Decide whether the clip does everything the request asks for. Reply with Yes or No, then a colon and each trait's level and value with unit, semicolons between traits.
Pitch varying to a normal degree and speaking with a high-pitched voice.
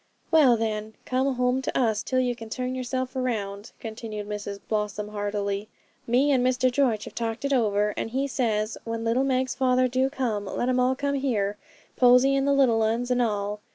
Yes: average, 3.3 semitones; high, 245 Hz